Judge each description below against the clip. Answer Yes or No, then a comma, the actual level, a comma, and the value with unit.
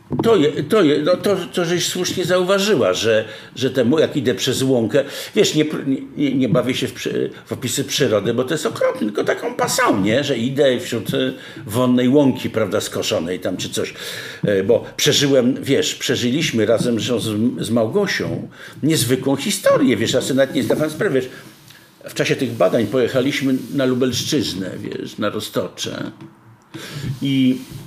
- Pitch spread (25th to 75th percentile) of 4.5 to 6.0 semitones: Yes, average, 5.2 semitones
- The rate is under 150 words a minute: No, fast, 160 wpm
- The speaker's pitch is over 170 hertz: No, medium, 140 Hz